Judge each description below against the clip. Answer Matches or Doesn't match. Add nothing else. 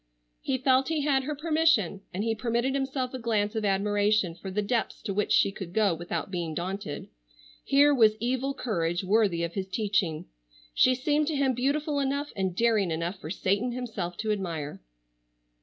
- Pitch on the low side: Doesn't match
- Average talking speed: Matches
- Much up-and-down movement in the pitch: Matches